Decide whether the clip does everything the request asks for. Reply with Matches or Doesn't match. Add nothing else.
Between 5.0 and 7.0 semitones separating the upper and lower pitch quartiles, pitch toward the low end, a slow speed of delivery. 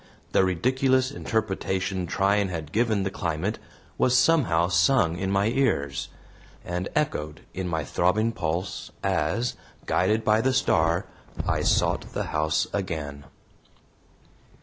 Matches